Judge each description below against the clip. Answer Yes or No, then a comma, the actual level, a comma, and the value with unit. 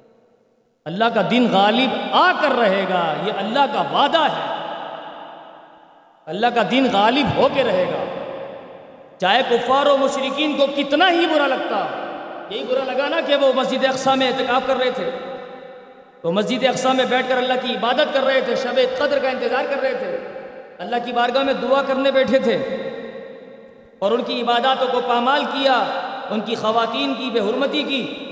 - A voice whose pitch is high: Yes, very high, 260 Hz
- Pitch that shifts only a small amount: Yes, narrow, 2.0 semitones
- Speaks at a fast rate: No, average, 180 wpm